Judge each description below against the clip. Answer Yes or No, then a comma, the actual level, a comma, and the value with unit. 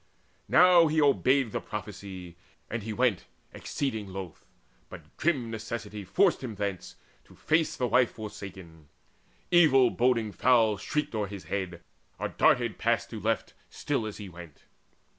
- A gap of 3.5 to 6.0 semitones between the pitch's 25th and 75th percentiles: Yes, average, 4.9 semitones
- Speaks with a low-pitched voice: Yes, low, 110 Hz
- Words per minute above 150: No, average, 145 wpm